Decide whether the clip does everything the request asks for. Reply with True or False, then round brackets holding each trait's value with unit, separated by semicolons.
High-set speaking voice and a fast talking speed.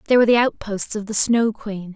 True (215 Hz; 245 wpm)